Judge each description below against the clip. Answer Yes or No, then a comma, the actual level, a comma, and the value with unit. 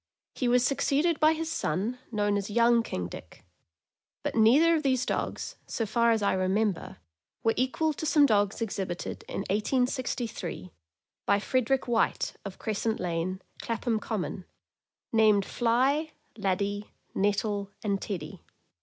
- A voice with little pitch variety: No, average, 4.1 semitones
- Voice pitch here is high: Yes, high, 220 Hz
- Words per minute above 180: No, slow, 135 wpm